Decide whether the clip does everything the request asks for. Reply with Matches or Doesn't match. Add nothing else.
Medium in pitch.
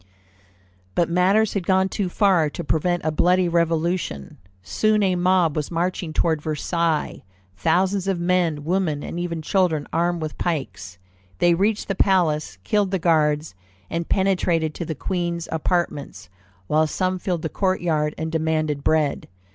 Matches